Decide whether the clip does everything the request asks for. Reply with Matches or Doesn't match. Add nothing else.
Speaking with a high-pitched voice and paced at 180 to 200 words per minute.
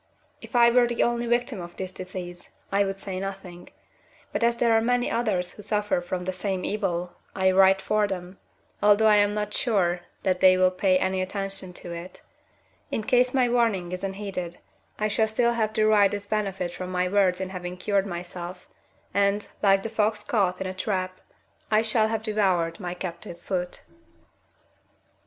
Matches